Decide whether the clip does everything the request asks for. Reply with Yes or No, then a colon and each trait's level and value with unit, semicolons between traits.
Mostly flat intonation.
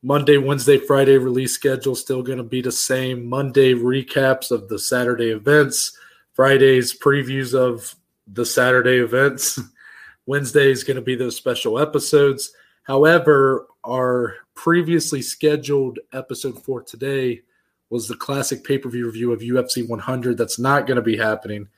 Yes: narrow, 2.0 semitones